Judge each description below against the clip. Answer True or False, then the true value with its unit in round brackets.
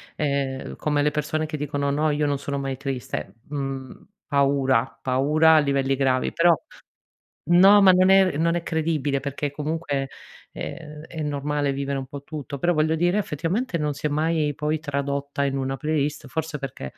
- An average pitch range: False (2.3 semitones)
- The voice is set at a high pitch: False (145 Hz)